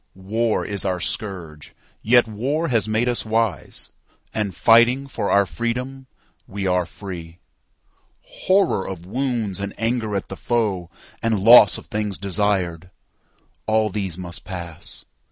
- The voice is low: Yes, low, 105 Hz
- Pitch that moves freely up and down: No, average, 3.9 semitones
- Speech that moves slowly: Yes, slow, 125 wpm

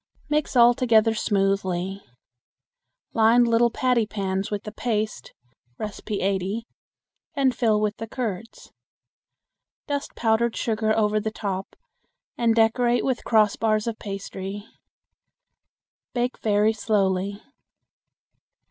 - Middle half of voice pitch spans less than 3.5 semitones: Yes, narrow, 2.6 semitones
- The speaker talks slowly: Yes, slow, 105 wpm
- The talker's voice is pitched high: Yes, high, 220 Hz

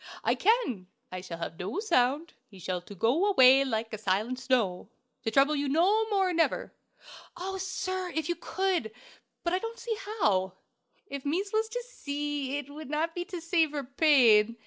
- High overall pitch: Yes, very high, 290 Hz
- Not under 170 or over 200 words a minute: Yes, average, 185 wpm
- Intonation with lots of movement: Yes, wide, 8.1 semitones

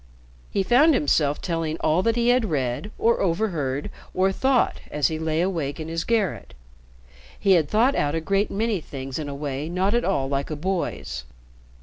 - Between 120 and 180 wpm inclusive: No, average, 190 wpm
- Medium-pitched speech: Yes, medium, 165 Hz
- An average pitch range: No, wide, 5.8 semitones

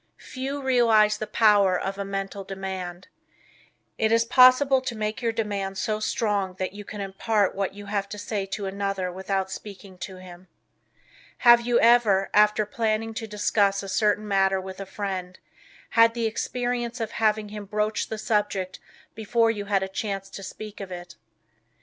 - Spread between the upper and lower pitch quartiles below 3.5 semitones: Yes, narrow, 2.5 semitones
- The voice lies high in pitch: Yes, high, 205 Hz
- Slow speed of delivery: No, average, 175 wpm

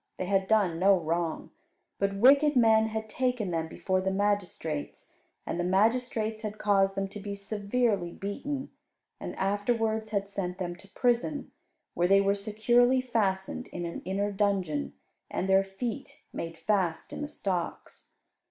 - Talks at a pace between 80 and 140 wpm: No, average, 155 wpm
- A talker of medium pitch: No, high, 200 Hz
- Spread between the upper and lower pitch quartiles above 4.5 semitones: No, average, 2.7 semitones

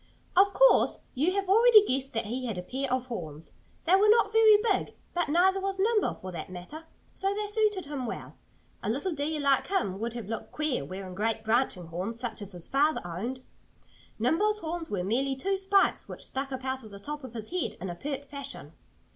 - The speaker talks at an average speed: No, fast, 215 wpm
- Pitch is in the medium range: No, very high, 270 Hz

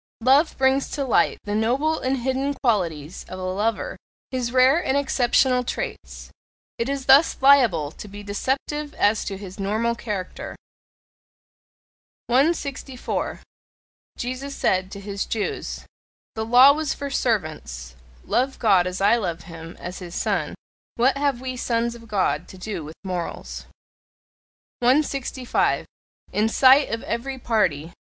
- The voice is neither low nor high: No, high, 235 Hz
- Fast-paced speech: No, average, 140 wpm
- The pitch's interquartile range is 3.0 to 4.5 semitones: No, wide, 5.5 semitones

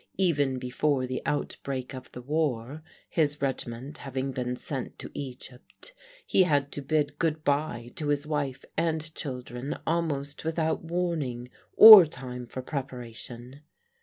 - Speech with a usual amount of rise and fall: Yes, average, 3.5 semitones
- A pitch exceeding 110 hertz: Yes, medium, 140 Hz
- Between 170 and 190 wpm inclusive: No, slow, 135 wpm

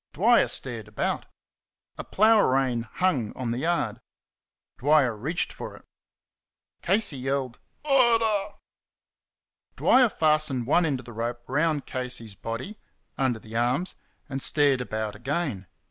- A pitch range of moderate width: No, wide, 6.2 semitones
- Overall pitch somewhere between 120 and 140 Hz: Yes, low, 135 Hz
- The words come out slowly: Yes, slow, 130 wpm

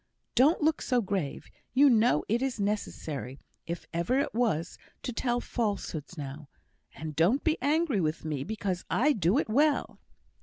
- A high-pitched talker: Yes, high, 210 Hz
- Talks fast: No, average, 160 wpm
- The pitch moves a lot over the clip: Yes, wide, 8.0 semitones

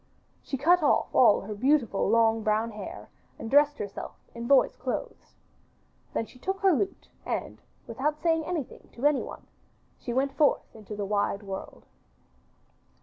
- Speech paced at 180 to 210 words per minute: No, average, 150 wpm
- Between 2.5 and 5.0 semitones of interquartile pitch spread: No, wide, 5.5 semitones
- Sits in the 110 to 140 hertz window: No, very high, 255 Hz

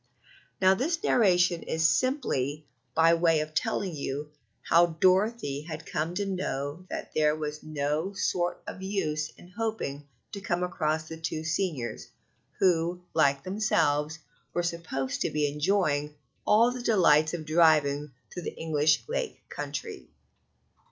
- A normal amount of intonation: Yes, average, 3.6 semitones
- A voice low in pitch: No, medium, 160 Hz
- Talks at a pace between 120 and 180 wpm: Yes, average, 140 wpm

